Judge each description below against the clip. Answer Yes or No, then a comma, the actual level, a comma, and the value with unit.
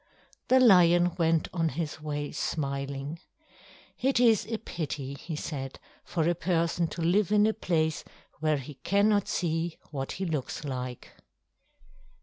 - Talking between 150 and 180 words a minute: No, average, 140 wpm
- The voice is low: No, medium, 165 Hz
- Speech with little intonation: No, average, 3.7 semitones